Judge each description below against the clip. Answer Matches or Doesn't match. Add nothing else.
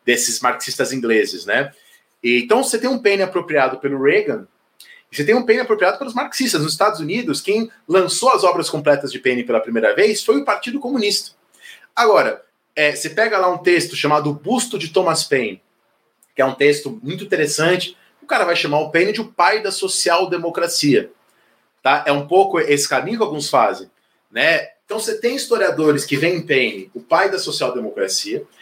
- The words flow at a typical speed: Doesn't match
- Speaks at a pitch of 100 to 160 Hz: Doesn't match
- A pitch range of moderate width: Doesn't match